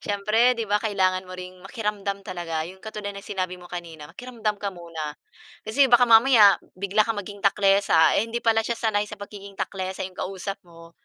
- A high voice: Yes, high, 200 Hz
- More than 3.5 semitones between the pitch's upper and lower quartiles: No, average, 2.8 semitones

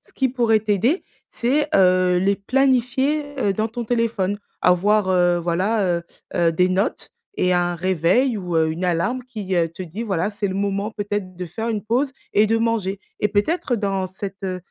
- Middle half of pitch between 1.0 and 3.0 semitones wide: No, average, 4.0 semitones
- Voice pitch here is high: Yes, high, 200 Hz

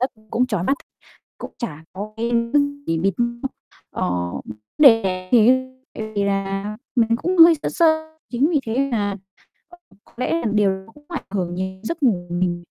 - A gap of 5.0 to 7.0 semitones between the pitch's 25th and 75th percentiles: Yes, wide, 5.6 semitones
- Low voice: No, high, 215 Hz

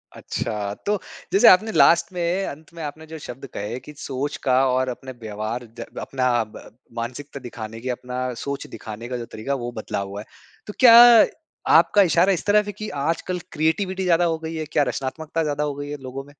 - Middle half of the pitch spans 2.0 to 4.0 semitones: No, average, 5.3 semitones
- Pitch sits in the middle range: Yes, medium, 145 Hz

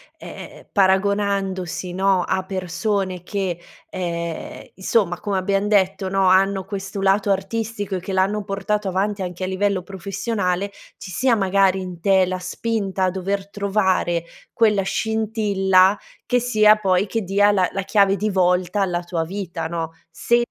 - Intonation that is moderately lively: No, narrow, 1.8 semitones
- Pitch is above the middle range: Yes, high, 195 Hz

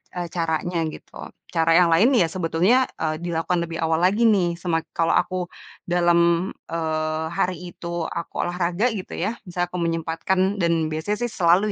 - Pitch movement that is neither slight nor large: No, narrow, 1.8 semitones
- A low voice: No, medium, 170 Hz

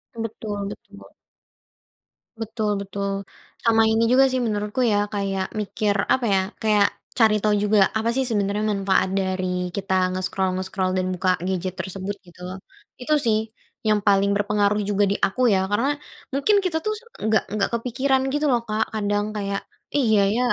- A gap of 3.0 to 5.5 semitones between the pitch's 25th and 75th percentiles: No, narrow, 2.5 semitones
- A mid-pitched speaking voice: No, high, 205 Hz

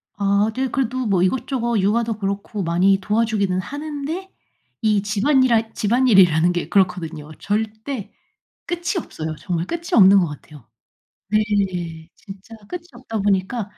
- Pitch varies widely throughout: No, average, 4.2 semitones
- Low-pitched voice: No, high, 205 Hz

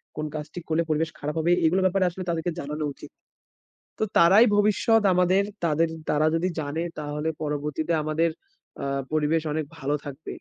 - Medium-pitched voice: Yes, medium, 160 Hz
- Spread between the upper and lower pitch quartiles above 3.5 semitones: No, average, 2.9 semitones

